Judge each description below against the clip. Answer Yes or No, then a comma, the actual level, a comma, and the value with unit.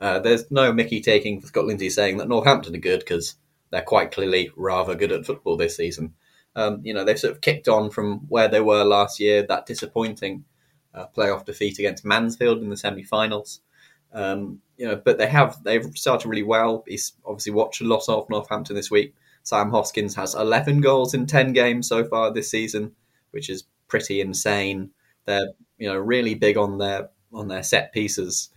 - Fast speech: No, average, 195 wpm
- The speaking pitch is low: Yes, low, 110 Hz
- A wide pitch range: No, average, 2.8 semitones